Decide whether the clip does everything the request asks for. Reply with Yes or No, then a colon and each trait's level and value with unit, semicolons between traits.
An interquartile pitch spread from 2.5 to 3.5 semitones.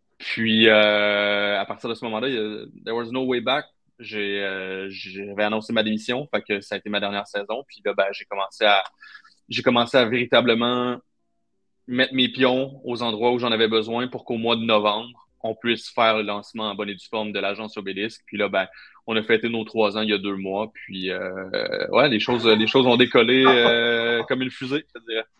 Yes: average, 2.8 semitones